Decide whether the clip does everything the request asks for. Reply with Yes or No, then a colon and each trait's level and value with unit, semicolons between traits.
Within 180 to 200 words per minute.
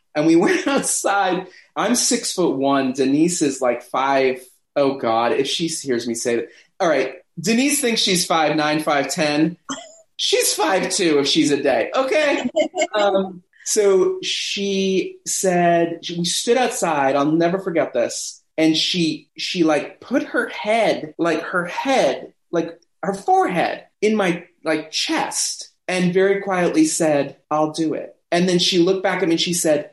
No: average, 165 wpm